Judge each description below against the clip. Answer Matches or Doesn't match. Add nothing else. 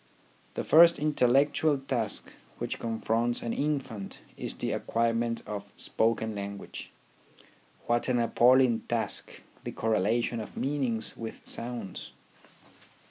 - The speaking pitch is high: Doesn't match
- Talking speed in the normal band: Doesn't match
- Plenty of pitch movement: Doesn't match